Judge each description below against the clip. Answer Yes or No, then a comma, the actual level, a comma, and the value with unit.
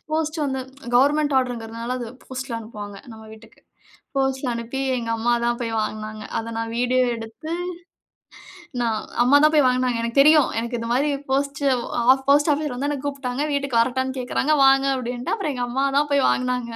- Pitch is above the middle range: Yes, very high, 255 Hz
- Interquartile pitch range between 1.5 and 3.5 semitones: Yes, average, 3.1 semitones